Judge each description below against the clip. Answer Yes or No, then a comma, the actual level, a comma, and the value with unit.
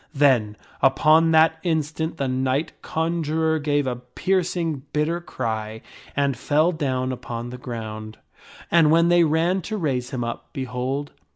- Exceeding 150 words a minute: No, average, 145 wpm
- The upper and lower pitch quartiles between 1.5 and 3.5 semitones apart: No, average, 4.4 semitones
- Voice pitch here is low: No, medium, 145 Hz